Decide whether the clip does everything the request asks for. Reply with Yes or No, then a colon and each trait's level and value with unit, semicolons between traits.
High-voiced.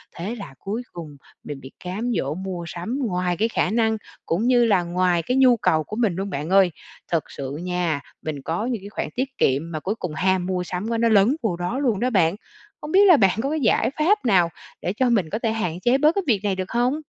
Yes: high, 195 Hz